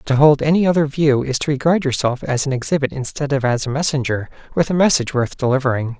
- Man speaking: Yes, male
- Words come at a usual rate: No, fast, 220 wpm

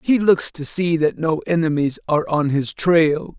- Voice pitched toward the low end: No, medium, 160 Hz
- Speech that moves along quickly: No, average, 195 wpm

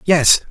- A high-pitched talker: No, medium, 150 Hz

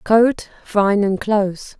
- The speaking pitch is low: No, high, 205 Hz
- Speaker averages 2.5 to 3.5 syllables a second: Yes, 3.1 syllables/s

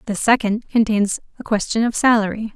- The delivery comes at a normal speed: Yes, average, 165 wpm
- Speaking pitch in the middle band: No, high, 220 Hz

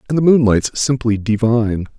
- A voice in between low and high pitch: No, low, 120 Hz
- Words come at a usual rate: Yes, average, 180 wpm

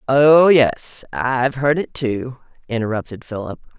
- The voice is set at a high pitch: No, low, 125 Hz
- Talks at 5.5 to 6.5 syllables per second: No, 4.2 syllables/s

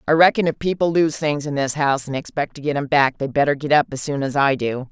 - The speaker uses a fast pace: Yes, fast, 295 wpm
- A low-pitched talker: No, medium, 145 Hz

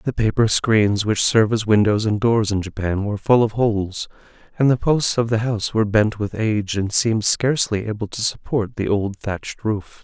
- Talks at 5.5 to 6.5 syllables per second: No, 5.3 syllables/s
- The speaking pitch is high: No, low, 110 Hz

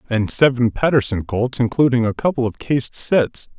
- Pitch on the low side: Yes, low, 125 Hz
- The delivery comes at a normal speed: Yes, average, 165 wpm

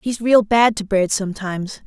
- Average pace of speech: Yes, average, 195 wpm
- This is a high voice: Yes, high, 210 Hz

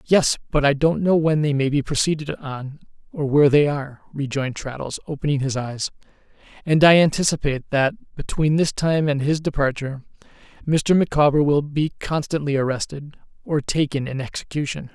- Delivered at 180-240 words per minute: No, average, 160 wpm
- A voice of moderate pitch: Yes, medium, 145 Hz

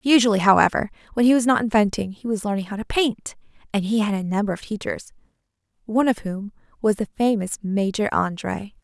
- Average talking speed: Yes, average, 190 wpm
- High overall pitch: Yes, high, 215 Hz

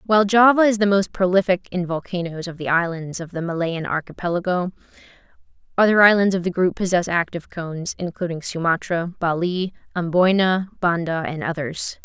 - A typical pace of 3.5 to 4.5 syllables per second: No, 5.5 syllables/s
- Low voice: No, medium, 180 Hz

